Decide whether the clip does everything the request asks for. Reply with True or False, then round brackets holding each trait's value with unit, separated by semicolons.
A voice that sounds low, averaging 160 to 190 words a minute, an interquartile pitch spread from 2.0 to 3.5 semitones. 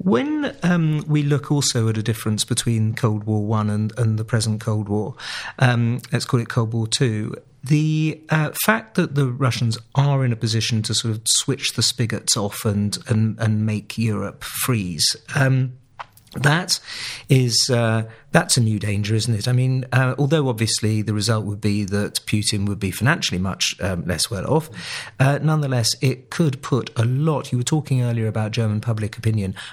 False (120 Hz; 180 wpm; 3.9 semitones)